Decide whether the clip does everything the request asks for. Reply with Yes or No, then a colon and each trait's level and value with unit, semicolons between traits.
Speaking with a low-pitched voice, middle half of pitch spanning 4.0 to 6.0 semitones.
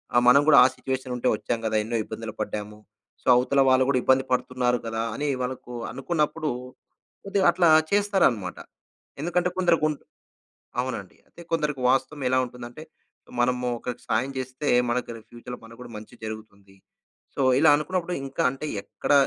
Yes: low, 130 Hz; average, 4.4 semitones